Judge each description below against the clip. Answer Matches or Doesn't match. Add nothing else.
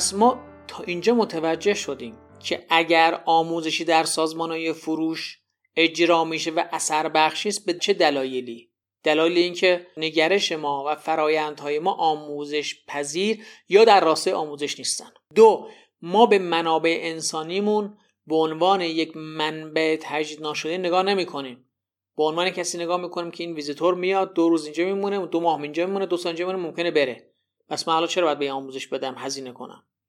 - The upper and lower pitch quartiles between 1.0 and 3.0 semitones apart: Matches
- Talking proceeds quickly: Matches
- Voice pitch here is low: Doesn't match